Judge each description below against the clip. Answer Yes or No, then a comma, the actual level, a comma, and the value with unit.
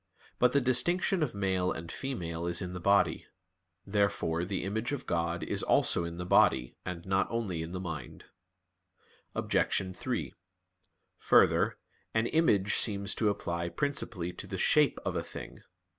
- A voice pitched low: Yes, very low, 95 Hz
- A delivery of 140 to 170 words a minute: Yes, average, 160 wpm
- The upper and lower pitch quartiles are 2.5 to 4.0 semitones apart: No, average, 4.6 semitones